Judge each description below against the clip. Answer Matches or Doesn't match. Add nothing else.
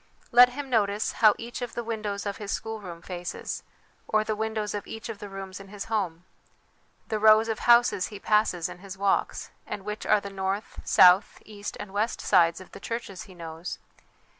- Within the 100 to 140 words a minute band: Doesn't match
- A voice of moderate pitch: Doesn't match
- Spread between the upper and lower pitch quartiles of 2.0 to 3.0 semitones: Matches